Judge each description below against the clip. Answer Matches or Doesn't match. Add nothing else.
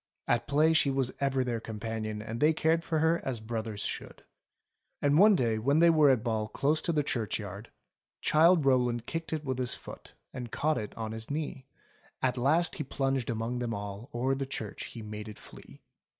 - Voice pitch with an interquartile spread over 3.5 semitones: Matches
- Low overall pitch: Matches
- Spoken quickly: Matches